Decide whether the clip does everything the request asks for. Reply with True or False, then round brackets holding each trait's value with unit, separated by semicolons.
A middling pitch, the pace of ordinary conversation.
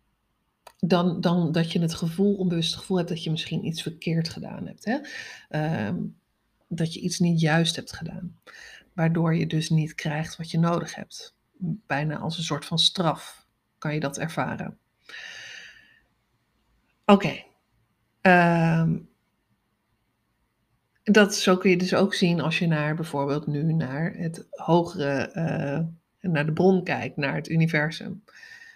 True (170 Hz; 150 wpm)